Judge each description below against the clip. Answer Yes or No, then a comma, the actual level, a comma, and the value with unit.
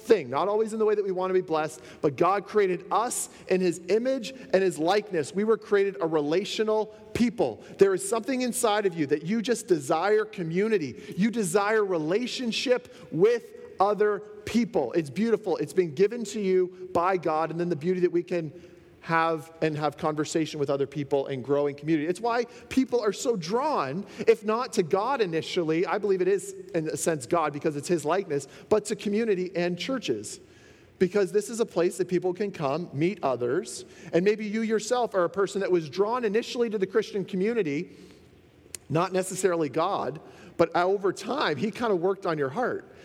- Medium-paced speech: Yes, average, 190 wpm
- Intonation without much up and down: No, average, 4.4 semitones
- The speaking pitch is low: No, high, 190 Hz